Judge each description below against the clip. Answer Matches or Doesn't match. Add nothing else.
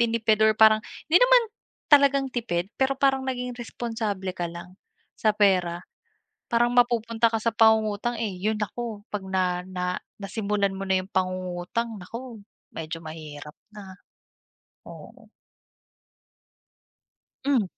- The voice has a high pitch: Matches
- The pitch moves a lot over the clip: Doesn't match